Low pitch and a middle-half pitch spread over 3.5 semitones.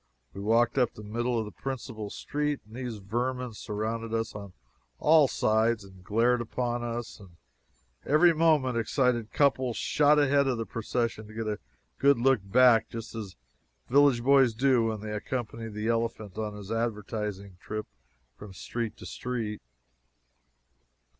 No: low, 115 Hz; average, 3.0 semitones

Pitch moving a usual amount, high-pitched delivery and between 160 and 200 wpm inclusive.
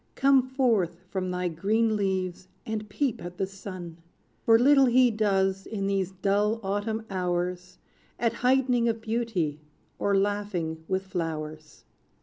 No: average, 3.8 semitones; high, 195 Hz; slow, 135 wpm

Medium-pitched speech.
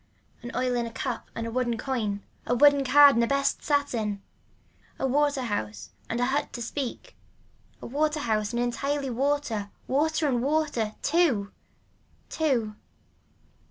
No: very high, 255 Hz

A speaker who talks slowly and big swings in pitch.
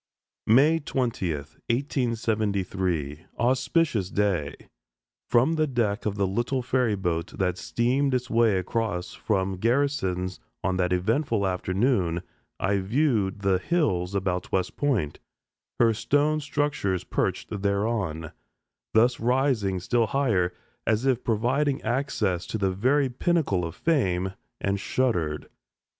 Yes: slow, 120 wpm; wide, 5.7 semitones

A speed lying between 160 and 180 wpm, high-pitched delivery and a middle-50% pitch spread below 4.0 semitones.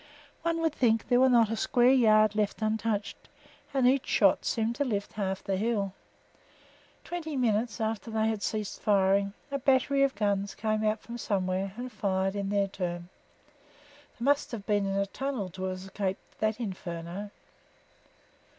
Yes: average, 170 wpm; high, 215 Hz; average, 3.5 semitones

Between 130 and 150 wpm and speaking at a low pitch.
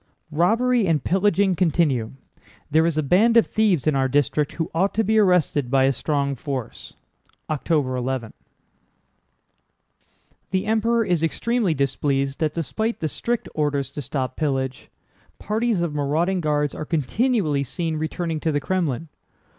No: average, 145 wpm; medium, 155 Hz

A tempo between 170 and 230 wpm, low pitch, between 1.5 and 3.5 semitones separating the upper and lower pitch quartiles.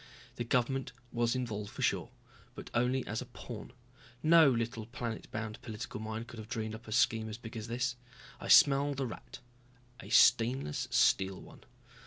Yes: average, 175 wpm; low, 115 Hz; narrow, 2.4 semitones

